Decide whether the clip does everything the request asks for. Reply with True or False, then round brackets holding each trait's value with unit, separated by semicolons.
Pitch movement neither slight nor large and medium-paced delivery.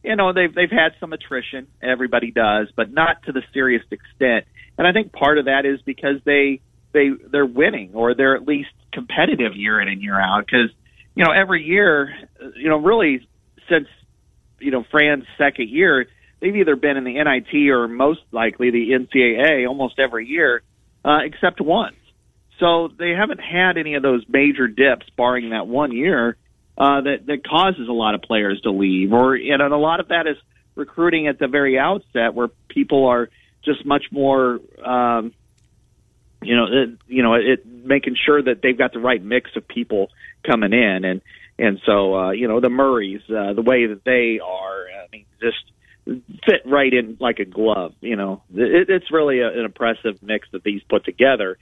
True (4.2 semitones; 190 wpm)